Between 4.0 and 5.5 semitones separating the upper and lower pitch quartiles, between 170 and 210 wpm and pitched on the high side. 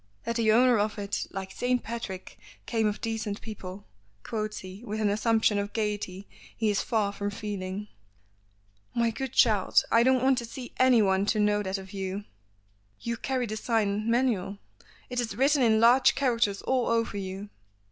No: narrow, 2.6 semitones; average, 175 wpm; high, 215 Hz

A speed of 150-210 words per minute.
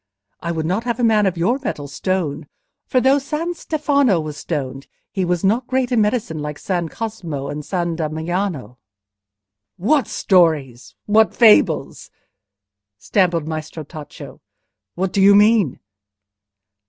No: average, 140 wpm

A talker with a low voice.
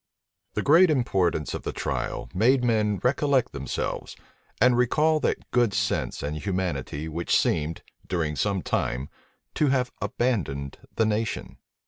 Yes: low, 105 Hz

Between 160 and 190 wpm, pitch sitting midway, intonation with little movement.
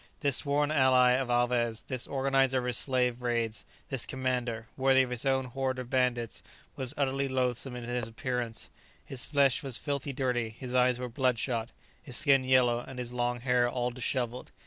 No: average, 180 wpm; low, 125 Hz; narrow, 1.5 semitones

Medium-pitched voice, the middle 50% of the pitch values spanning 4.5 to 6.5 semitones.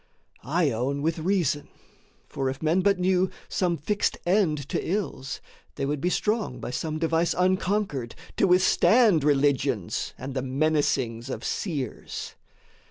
Yes: medium, 155 Hz; average, 5.2 semitones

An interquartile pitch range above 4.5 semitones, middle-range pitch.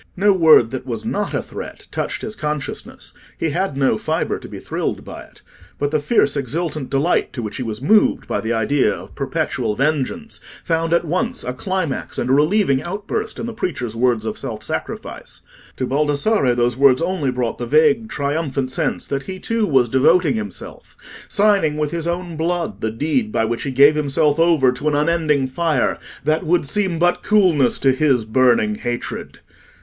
Yes: average, 5.3 semitones; medium, 150 Hz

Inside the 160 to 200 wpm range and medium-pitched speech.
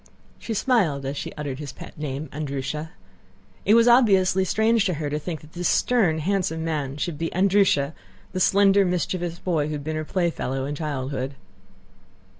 Yes: average, 170 wpm; medium, 160 Hz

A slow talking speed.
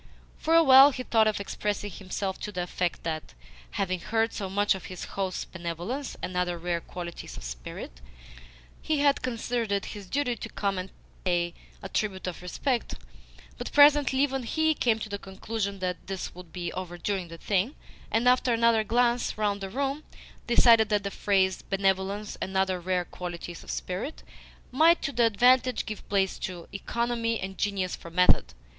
No: average, 175 wpm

